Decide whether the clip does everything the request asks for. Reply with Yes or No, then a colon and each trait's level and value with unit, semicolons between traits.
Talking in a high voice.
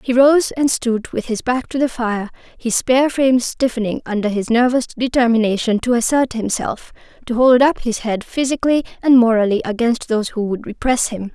Yes: high, 240 Hz